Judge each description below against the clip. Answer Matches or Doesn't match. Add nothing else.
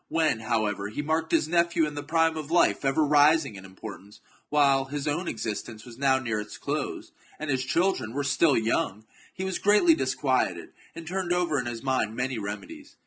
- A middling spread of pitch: Doesn't match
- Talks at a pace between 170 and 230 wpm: Matches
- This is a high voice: Doesn't match